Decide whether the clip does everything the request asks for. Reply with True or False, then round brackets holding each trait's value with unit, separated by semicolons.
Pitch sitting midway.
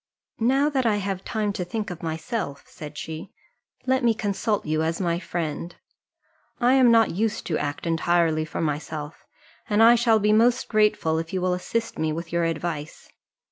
True (180 Hz)